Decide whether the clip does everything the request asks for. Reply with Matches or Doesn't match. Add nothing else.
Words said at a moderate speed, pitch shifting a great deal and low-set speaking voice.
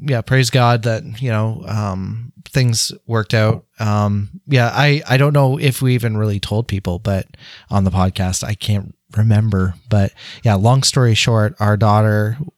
Doesn't match